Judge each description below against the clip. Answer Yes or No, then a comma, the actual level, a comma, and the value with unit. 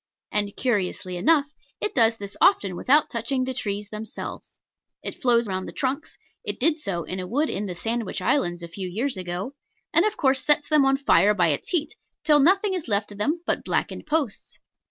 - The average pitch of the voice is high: Yes, high, 235 Hz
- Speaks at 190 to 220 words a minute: Yes, average, 200 wpm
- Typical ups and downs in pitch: No, wide, 6.8 semitones